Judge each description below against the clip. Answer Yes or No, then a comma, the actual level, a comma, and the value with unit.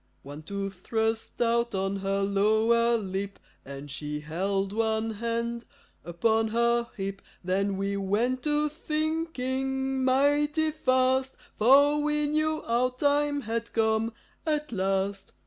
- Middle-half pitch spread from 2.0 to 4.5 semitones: No, average, 5.2 semitones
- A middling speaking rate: No, slow, 125 wpm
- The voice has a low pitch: No, high, 230 Hz